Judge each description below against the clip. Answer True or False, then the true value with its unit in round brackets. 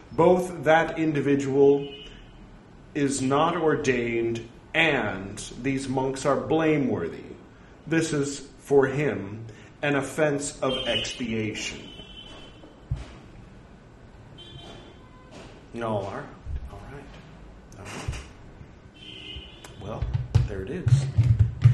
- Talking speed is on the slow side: True (85 wpm)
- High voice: False (135 Hz)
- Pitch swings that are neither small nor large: True (4.0 semitones)